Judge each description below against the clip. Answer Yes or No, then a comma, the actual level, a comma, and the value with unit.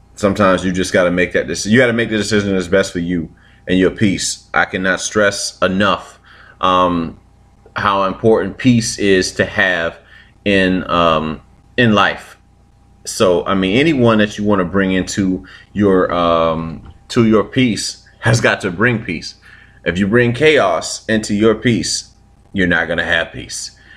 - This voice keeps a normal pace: Yes, average, 175 wpm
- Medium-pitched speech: No, very low, 95 Hz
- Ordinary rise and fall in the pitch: Yes, average, 3.1 semitones